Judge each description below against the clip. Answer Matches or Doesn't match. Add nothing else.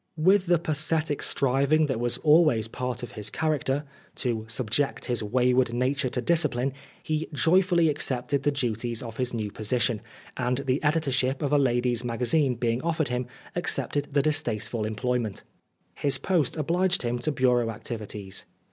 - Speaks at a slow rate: Doesn't match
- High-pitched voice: Doesn't match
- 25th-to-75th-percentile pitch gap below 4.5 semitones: Matches